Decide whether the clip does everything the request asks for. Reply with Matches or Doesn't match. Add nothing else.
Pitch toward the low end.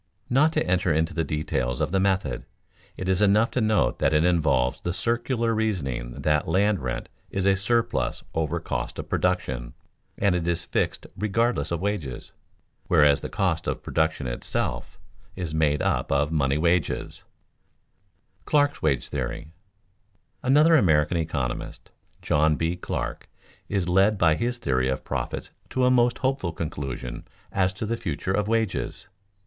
Matches